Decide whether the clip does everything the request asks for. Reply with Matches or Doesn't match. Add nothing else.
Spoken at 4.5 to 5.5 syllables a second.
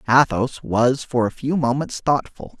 Doesn't match